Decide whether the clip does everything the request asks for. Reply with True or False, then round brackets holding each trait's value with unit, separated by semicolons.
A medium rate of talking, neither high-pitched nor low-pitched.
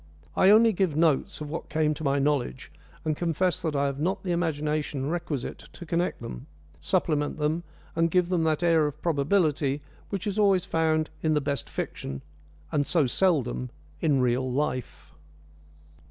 True (170 wpm; 155 Hz)